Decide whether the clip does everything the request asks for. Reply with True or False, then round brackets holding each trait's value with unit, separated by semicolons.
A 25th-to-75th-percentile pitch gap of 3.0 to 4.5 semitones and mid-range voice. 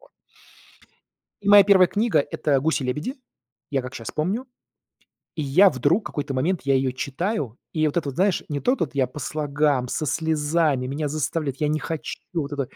True (3.7 semitones; 150 Hz)